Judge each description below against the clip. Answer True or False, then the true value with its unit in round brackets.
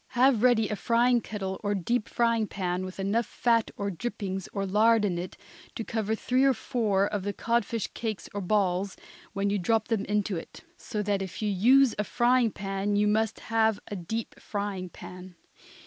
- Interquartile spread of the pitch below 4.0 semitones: True (2.8 semitones)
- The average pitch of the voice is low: False (210 Hz)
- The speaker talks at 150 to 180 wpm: False (190 wpm)